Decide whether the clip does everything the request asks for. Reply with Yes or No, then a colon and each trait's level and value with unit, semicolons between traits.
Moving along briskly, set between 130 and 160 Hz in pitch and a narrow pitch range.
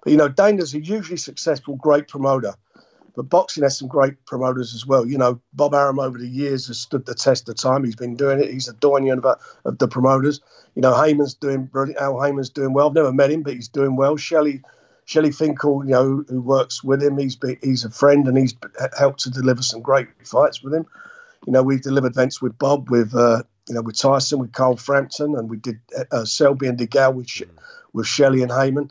Yes: fast, 230 wpm; low, 135 Hz; narrow, 2.0 semitones